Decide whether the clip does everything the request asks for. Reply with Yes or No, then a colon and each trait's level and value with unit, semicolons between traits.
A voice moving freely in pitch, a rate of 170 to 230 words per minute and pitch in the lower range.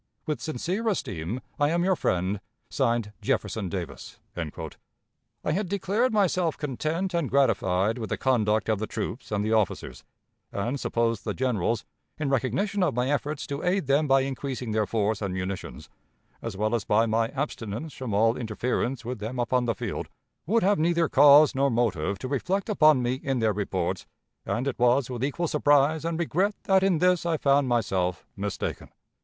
Yes: wide, 6.1 semitones; average, 175 wpm; low, 130 Hz